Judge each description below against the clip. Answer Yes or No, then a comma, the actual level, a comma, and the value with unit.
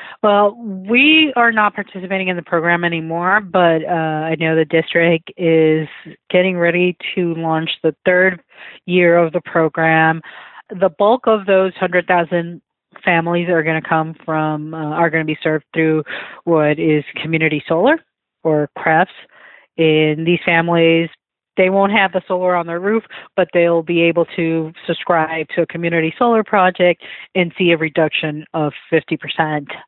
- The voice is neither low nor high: Yes, medium, 170 Hz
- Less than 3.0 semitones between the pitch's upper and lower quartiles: Yes, narrow, 2.5 semitones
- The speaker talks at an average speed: Yes, average, 155 wpm